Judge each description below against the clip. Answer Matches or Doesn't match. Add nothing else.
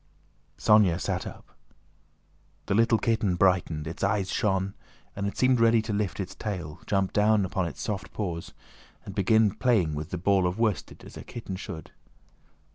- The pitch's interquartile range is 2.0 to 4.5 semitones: Matches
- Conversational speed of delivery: Matches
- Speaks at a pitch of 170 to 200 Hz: Doesn't match